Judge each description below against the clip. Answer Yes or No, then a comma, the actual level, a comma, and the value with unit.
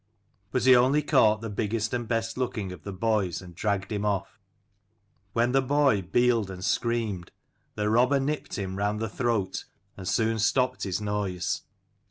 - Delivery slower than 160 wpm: No, average, 170 wpm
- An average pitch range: Yes, average, 3.5 semitones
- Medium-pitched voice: No, low, 110 Hz